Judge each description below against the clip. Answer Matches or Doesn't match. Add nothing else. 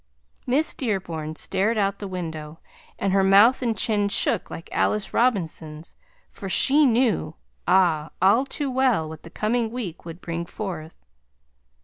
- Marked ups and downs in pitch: Matches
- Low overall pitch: Doesn't match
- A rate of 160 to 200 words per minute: Doesn't match